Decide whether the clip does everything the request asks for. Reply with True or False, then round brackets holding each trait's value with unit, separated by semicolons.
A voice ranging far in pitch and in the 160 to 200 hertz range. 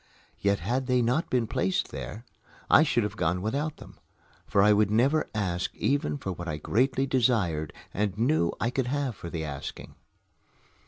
False (5.9 semitones; 110 Hz)